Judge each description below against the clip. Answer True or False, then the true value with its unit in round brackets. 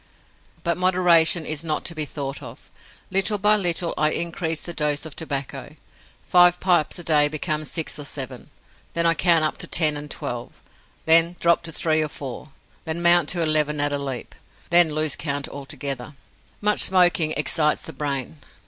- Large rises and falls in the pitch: False (2.8 semitones)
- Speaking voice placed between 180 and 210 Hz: False (155 Hz)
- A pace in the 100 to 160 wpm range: False (175 wpm)